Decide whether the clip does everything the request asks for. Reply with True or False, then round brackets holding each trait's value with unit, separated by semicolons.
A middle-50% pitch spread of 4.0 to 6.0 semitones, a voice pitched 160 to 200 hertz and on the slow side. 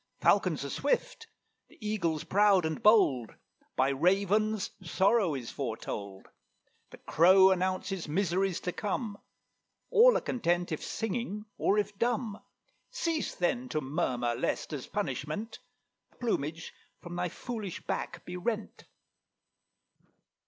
True (5.0 semitones; 190 Hz; 125 wpm)